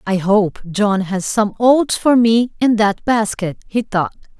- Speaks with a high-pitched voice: Yes, high, 215 Hz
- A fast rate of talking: No, average, 180 wpm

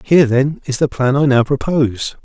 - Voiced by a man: Yes, male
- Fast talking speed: Yes, fast, 215 wpm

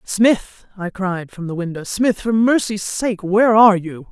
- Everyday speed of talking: Yes, average, 190 wpm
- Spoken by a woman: Yes, female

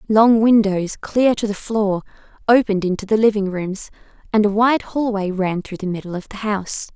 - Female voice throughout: Yes, female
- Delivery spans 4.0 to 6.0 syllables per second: Yes, 5.2 syllables/s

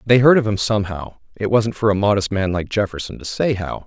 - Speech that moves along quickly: Yes, fast, 235 wpm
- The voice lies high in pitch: No, low, 105 Hz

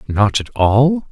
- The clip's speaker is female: No, male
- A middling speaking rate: Yes, average, 160 wpm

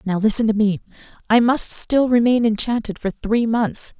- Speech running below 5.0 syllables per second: Yes, 4.7 syllables/s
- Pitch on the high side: Yes, high, 220 Hz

